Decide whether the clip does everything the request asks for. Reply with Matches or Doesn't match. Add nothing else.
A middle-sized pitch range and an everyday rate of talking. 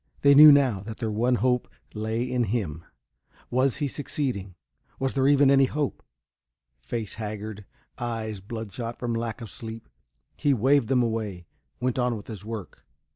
Matches